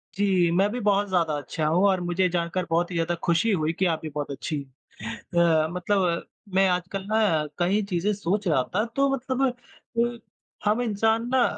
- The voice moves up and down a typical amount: Yes, average, 3.6 semitones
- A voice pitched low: No, medium, 185 Hz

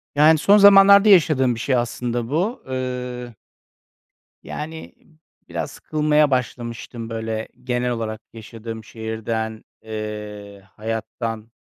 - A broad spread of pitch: No, average, 5.0 semitones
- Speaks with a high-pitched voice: No, low, 120 Hz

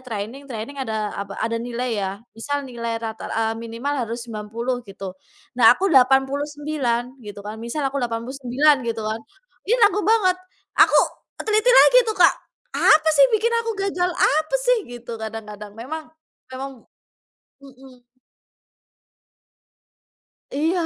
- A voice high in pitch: Yes, very high, 255 Hz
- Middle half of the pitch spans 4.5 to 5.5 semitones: Yes, average, 5.0 semitones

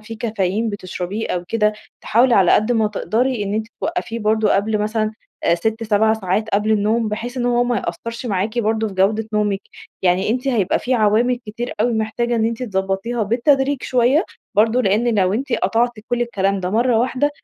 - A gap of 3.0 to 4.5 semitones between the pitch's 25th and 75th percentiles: No, narrow, 2.6 semitones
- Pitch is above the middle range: Yes, high, 220 Hz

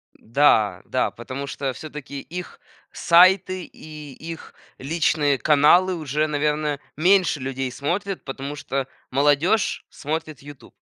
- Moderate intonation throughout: Yes, average, 3.2 semitones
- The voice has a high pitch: No, medium, 150 Hz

